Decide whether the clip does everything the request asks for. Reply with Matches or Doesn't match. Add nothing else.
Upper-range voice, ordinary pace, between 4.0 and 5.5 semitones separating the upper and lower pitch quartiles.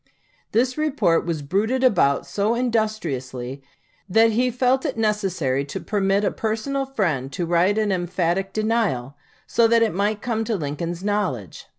Matches